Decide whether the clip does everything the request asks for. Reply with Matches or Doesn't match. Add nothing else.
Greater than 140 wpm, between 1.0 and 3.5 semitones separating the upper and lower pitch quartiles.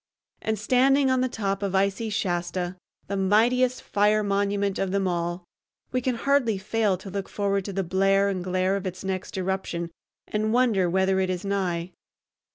Matches